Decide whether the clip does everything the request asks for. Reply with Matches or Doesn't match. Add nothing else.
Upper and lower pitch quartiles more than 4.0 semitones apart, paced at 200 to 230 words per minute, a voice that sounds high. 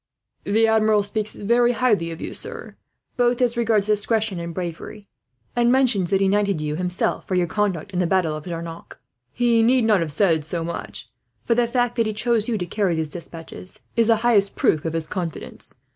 Matches